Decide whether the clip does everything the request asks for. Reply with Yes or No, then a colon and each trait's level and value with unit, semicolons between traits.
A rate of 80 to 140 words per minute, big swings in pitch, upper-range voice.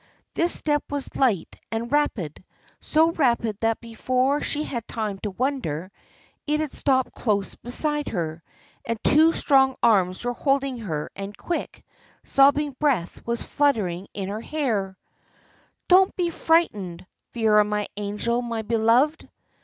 Yes: slow, 135 wpm; wide, 5.7 semitones; high, 235 Hz